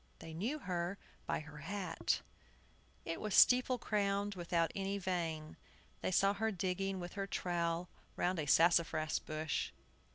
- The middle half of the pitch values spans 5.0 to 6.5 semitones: No, average, 3.1 semitones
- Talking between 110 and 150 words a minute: Yes, average, 140 wpm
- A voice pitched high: No, medium, 180 Hz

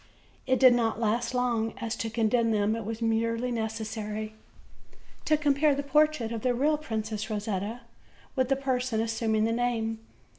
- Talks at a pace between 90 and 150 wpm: No, average, 160 wpm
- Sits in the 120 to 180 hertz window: No, high, 230 Hz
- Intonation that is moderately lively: No, narrow, 2.3 semitones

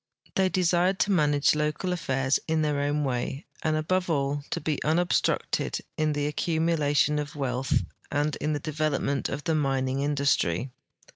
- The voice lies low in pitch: No, medium, 150 Hz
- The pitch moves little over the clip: Yes, narrow, 2.1 semitones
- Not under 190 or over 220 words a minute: No, average, 155 wpm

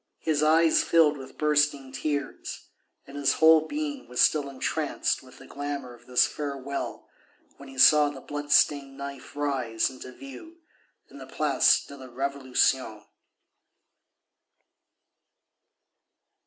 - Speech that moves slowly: Yes, slow, 130 wpm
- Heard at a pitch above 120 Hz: Yes, medium, 140 Hz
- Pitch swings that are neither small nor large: No, narrow, 2.3 semitones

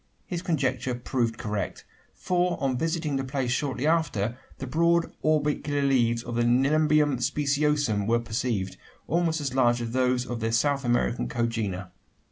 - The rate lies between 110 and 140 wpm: No, average, 150 wpm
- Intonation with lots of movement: No, average, 4.1 semitones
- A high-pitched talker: No, low, 130 Hz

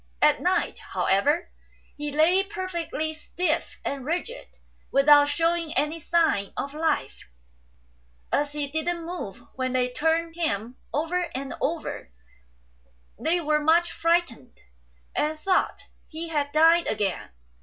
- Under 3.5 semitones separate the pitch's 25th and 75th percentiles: Yes, average, 2.9 semitones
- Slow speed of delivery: Yes, slow, 130 wpm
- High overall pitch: Yes, very high, 315 Hz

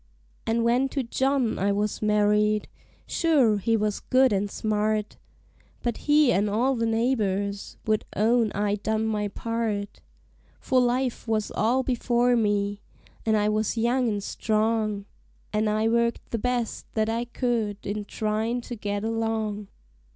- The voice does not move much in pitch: Yes, narrow, 2.3 semitones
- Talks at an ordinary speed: Yes, average, 150 wpm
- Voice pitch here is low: No, high, 220 Hz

